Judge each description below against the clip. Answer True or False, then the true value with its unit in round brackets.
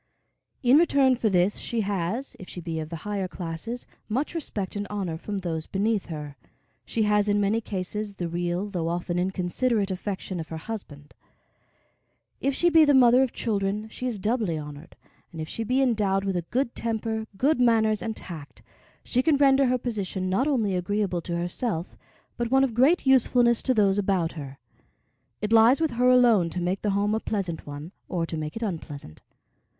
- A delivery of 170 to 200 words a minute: True (190 wpm)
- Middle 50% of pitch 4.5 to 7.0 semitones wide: True (5.2 semitones)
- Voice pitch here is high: True (205 Hz)